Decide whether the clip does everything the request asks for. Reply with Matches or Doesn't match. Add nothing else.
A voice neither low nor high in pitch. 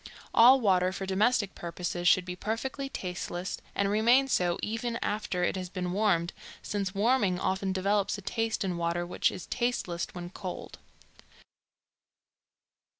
Doesn't match